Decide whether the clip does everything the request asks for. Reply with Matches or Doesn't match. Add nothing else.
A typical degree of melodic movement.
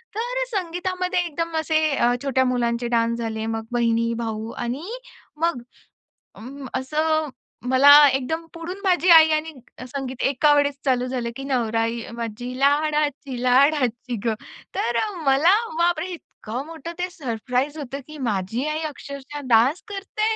Matches